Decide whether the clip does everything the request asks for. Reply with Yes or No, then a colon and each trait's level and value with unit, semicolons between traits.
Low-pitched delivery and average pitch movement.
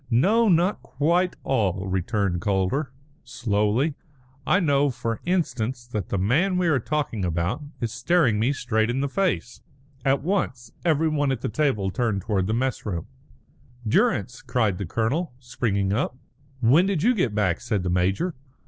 No: low, 120 Hz; wide, 6.7 semitones